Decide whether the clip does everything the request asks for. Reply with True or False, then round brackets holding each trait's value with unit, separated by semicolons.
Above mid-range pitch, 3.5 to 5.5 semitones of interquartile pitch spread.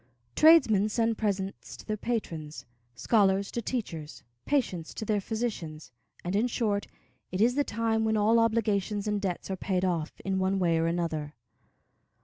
True (205 Hz; 3.8 semitones)